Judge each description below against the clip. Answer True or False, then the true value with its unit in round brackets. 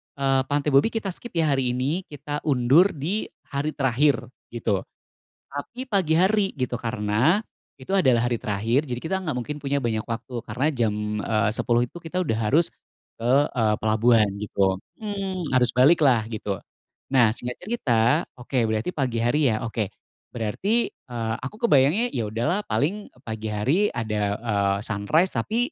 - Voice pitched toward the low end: True (130 Hz)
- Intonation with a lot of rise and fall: True (5.8 semitones)